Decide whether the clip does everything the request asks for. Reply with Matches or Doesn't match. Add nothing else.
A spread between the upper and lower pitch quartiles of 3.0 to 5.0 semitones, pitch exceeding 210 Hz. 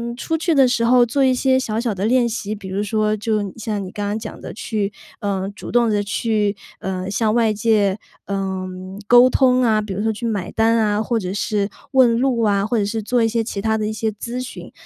Doesn't match